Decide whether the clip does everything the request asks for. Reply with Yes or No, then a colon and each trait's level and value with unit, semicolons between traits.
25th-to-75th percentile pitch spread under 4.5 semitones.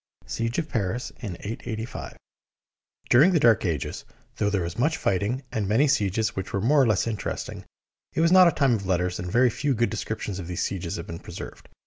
No: average, 5.1 semitones